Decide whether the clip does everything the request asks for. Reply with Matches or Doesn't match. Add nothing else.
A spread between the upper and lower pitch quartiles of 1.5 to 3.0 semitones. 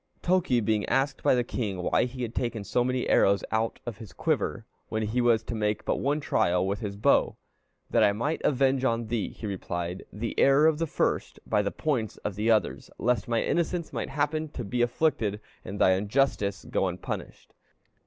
Doesn't match